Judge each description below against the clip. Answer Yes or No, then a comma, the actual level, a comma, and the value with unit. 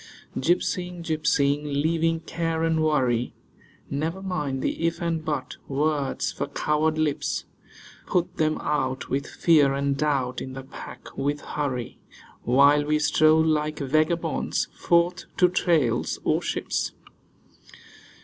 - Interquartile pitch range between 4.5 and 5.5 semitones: No, average, 2.8 semitones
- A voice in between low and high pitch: Yes, medium, 150 Hz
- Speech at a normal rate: No, slow, 125 wpm